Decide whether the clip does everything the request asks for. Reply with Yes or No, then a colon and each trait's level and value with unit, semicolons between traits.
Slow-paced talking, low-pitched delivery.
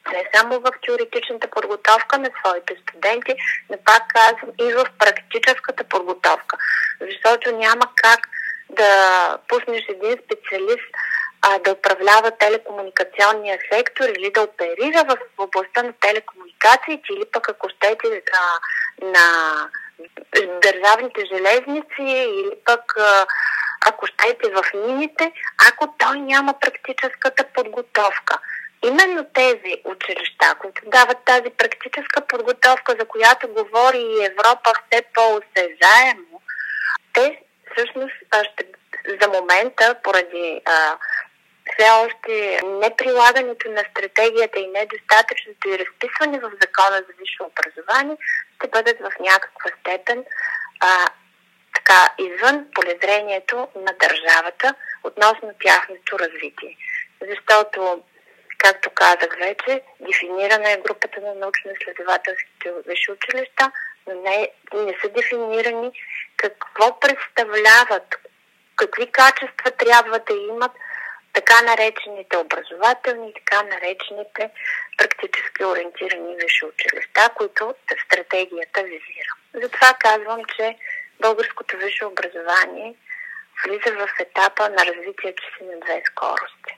No: slow, 105 wpm; high, 235 Hz